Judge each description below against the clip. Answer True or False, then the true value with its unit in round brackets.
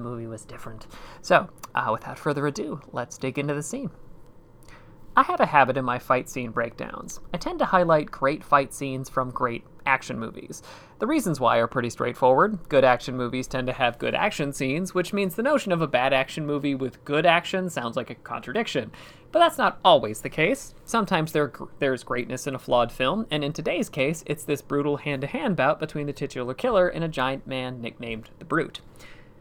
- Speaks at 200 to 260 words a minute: True (205 wpm)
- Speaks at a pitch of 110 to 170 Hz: True (140 Hz)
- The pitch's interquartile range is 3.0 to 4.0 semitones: True (3.7 semitones)